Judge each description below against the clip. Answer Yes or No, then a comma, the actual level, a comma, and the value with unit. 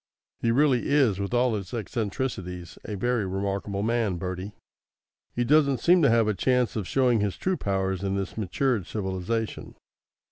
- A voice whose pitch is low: Yes, low, 110 Hz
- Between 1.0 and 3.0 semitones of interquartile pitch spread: No, average, 4.3 semitones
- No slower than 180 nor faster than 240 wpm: No, average, 165 wpm